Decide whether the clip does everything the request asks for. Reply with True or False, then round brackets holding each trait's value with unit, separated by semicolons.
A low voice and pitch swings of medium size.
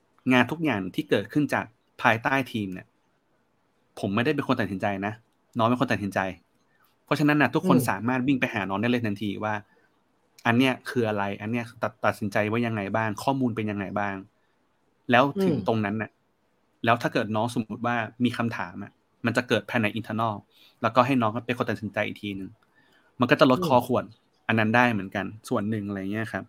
True (110 Hz; 3.2 semitones)